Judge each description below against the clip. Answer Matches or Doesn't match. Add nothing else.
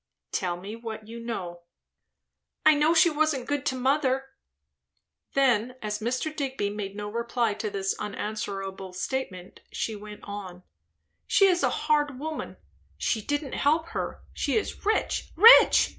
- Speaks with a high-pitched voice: Matches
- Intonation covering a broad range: Matches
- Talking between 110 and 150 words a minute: Matches